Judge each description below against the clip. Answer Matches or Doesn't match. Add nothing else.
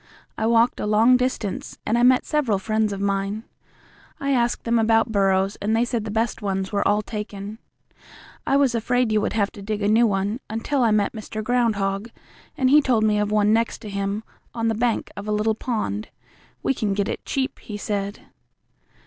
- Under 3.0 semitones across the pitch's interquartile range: Matches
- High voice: Matches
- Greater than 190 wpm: Matches